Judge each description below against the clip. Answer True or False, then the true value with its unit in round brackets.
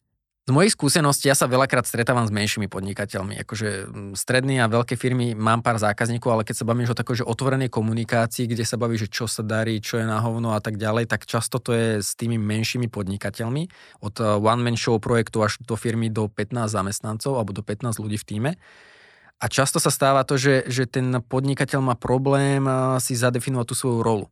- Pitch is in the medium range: False (120 Hz)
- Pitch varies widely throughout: False (2.9 semitones)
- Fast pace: True (200 wpm)